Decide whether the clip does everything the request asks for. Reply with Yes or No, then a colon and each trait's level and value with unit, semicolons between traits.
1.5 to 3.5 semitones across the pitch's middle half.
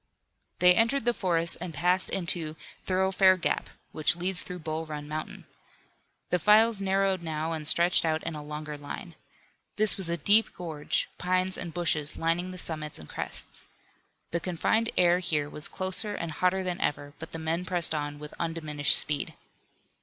Yes: average, 3.2 semitones